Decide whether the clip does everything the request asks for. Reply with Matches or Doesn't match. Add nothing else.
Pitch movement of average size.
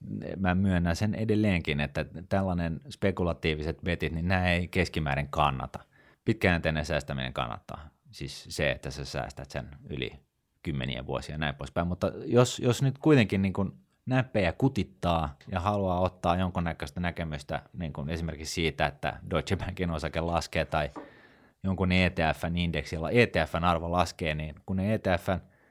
Matches